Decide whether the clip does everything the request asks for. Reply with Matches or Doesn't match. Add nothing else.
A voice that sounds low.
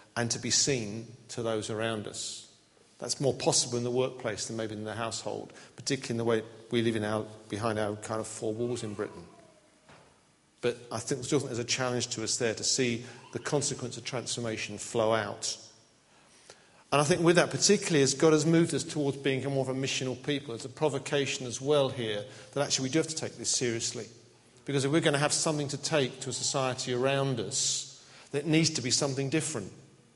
Matches